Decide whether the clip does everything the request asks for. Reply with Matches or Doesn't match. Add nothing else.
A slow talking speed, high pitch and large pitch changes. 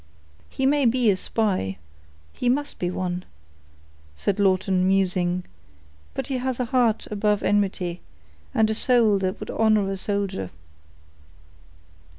Doesn't match